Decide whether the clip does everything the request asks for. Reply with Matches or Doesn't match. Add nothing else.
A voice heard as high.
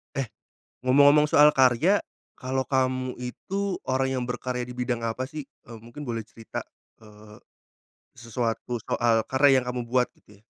Doesn't match